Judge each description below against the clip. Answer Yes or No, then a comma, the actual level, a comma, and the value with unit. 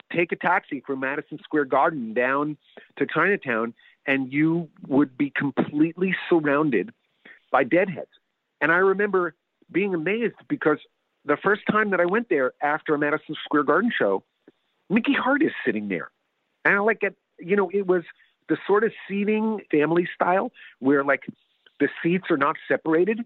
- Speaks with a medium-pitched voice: Yes, medium, 170 Hz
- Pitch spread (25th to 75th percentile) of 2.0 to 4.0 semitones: No, wide, 5.5 semitones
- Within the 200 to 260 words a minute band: No, average, 160 wpm